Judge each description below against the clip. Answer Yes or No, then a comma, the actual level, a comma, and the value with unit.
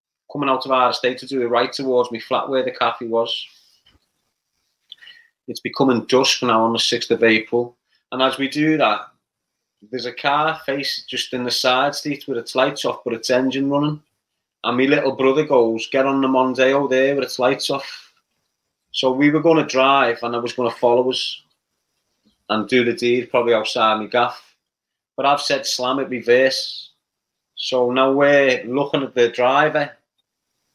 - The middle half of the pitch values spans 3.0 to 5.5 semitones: No, narrow, 2.5 semitones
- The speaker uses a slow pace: No, average, 180 wpm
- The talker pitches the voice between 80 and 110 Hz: No, low, 130 Hz